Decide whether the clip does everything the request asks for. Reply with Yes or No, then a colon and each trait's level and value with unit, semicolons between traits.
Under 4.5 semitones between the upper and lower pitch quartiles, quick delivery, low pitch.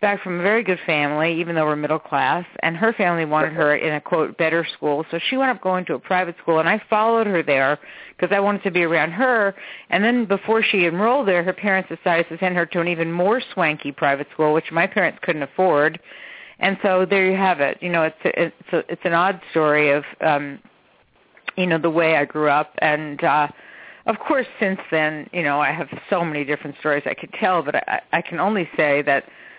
No: average, 3.9 semitones; fast, 235 wpm; medium, 170 Hz